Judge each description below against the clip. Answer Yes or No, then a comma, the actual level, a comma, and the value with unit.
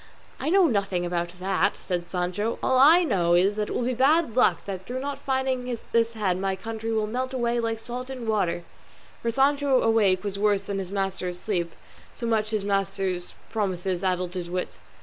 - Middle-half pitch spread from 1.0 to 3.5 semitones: No, average, 4.7 semitones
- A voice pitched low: No, high, 210 Hz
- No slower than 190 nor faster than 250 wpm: Yes, average, 200 wpm